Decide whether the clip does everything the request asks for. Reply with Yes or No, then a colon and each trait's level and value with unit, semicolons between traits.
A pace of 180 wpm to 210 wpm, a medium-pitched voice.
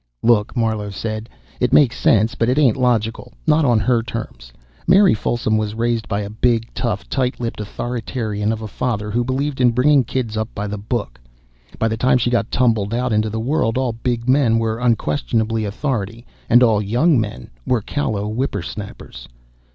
No: average, 185 wpm; low, 115 Hz